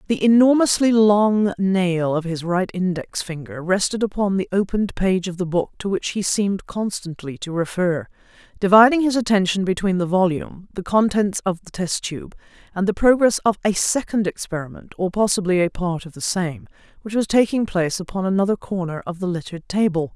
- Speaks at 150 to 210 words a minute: Yes, average, 180 wpm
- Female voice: Yes, female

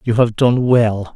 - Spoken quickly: Yes, fast, 210 wpm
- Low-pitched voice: Yes, low, 115 Hz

